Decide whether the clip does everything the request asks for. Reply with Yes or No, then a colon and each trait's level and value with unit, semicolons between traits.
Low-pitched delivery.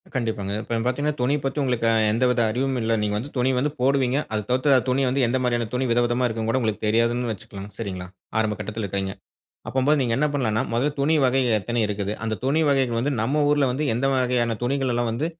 Yes: low, 125 Hz